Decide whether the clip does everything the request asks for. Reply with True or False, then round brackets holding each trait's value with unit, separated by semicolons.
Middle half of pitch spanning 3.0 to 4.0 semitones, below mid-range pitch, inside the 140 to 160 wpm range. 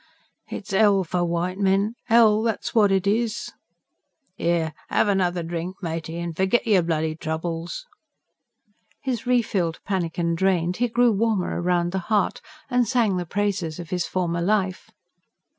False (3.7 semitones; 185 Hz; 150 wpm)